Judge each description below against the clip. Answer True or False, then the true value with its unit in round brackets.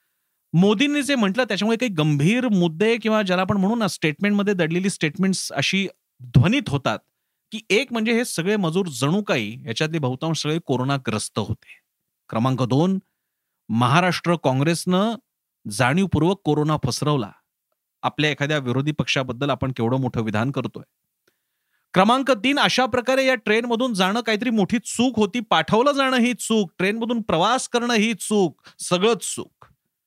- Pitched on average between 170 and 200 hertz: True (185 Hz)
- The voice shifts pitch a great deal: True (7.0 semitones)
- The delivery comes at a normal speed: False (135 wpm)